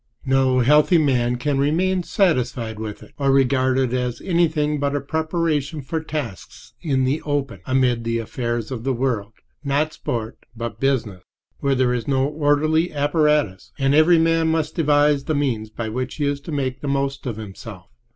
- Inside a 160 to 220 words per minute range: Yes, average, 170 wpm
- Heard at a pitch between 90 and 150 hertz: Yes, low, 135 Hz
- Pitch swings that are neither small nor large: Yes, average, 3.6 semitones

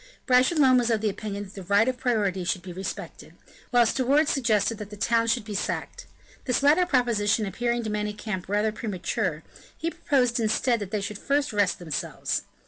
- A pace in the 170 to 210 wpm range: Yes, average, 190 wpm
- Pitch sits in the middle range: No, high, 220 Hz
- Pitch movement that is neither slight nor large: Yes, average, 3.6 semitones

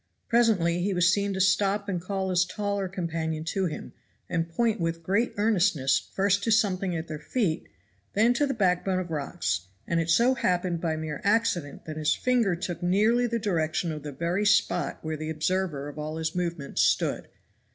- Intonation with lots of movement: No, average, 4.0 semitones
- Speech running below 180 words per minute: No, average, 190 wpm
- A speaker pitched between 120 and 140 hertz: No, medium, 180 Hz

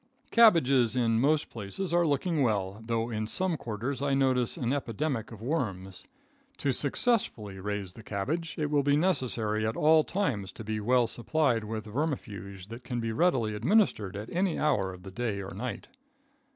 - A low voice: Yes, low, 120 Hz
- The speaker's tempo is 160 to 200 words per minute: Yes, average, 175 wpm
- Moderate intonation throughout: No, wide, 5.7 semitones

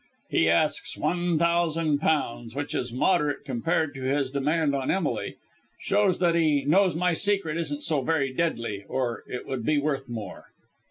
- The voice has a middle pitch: Yes, medium, 150 Hz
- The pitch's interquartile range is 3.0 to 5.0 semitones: Yes, average, 4.1 semitones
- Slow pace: No, average, 165 wpm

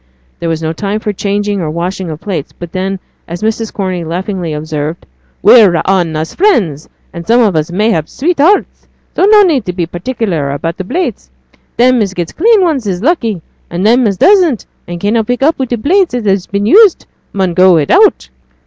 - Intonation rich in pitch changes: Yes, wide, 6.1 semitones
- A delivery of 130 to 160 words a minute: No, average, 195 wpm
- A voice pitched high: Yes, high, 195 Hz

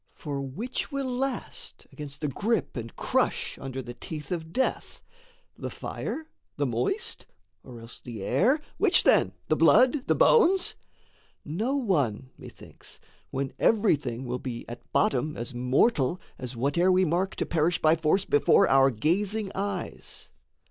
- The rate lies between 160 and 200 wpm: No, average, 150 wpm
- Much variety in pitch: Yes, wide, 7.9 semitones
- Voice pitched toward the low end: No, medium, 155 Hz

